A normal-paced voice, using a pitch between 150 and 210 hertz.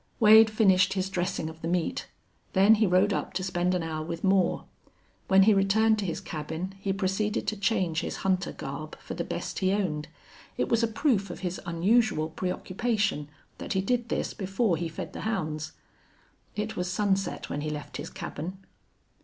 Yes: average, 185 wpm; high, 190 Hz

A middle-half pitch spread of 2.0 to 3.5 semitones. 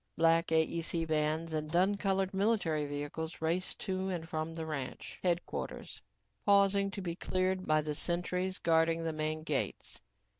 Yes: average, 2.9 semitones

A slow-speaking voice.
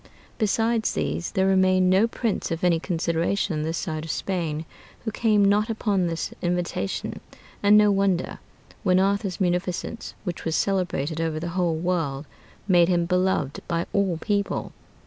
No: average, 155 wpm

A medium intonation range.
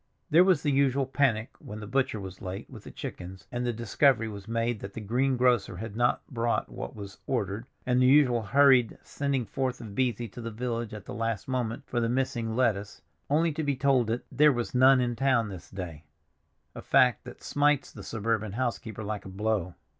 Yes: average, 3.7 semitones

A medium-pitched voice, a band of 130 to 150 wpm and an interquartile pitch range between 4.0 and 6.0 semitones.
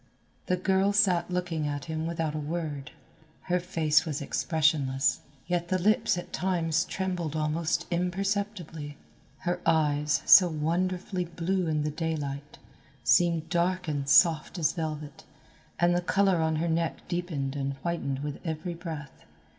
No: medium, 165 Hz; average, 145 wpm; average, 2.9 semitones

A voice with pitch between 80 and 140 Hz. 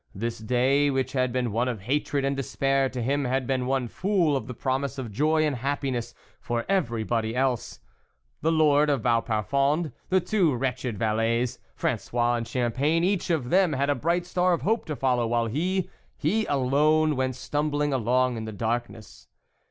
Yes: low, 135 Hz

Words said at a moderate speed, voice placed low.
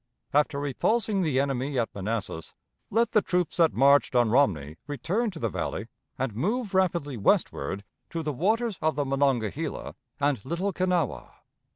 No: average, 155 wpm; medium, 145 Hz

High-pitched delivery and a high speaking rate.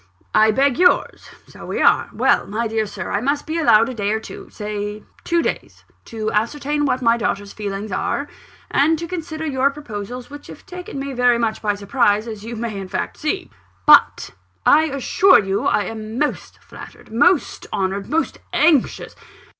No: high, 235 Hz; average, 180 wpm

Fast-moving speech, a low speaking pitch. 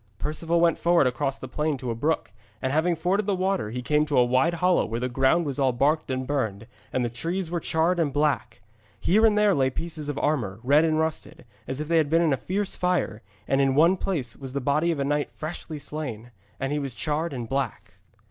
No: fast, 235 wpm; medium, 150 Hz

